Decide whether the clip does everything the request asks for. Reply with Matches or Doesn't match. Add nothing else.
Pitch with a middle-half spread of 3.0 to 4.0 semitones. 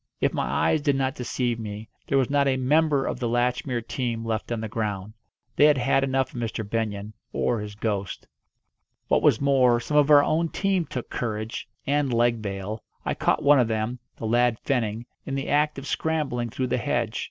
Matches